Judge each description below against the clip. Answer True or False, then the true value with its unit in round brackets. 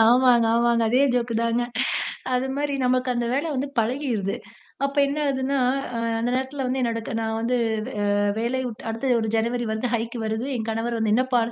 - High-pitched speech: True (240 Hz)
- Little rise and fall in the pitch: True (2.3 semitones)